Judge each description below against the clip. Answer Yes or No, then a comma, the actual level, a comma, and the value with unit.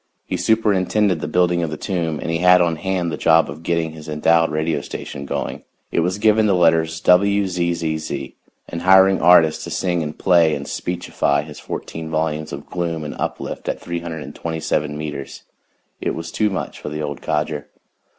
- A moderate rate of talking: Yes, average, 180 wpm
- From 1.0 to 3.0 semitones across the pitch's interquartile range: Yes, narrow, 2.6 semitones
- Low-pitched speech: Yes, very low, 80 Hz